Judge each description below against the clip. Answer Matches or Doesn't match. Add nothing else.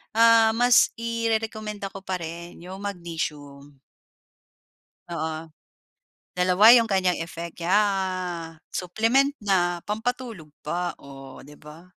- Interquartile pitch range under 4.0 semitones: Doesn't match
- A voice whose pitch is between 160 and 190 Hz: Matches